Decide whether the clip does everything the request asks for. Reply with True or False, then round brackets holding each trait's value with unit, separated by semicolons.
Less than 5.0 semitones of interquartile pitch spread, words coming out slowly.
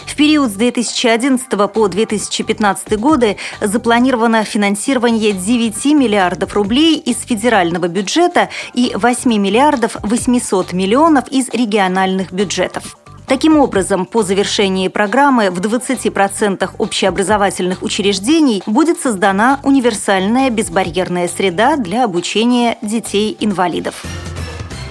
True (4.0 semitones; 95 wpm)